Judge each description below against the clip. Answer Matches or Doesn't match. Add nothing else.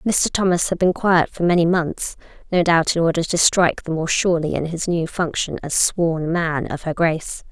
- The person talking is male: Doesn't match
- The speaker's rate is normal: Doesn't match